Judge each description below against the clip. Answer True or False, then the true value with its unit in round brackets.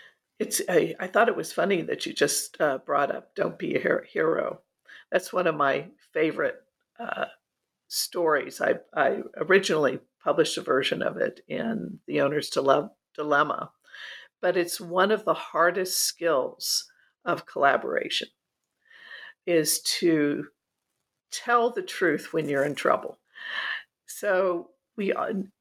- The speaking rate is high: False (135 wpm)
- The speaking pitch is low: False (235 Hz)